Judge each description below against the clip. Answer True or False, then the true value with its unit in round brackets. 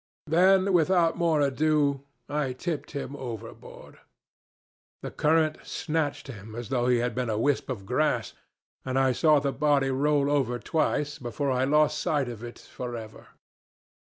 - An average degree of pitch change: True (3.5 semitones)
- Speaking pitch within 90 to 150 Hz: True (140 Hz)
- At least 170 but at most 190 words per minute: False (155 wpm)